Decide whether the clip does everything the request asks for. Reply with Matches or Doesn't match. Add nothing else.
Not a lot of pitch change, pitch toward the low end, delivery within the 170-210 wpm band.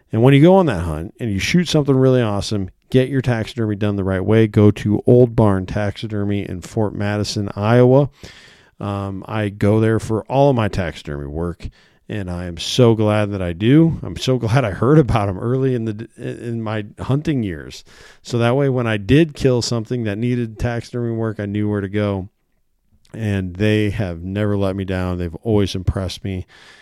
Doesn't match